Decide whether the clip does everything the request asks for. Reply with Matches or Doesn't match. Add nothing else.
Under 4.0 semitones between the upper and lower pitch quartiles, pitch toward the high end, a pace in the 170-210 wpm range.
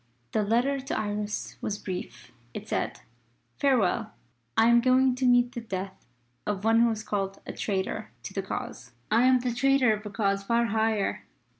Matches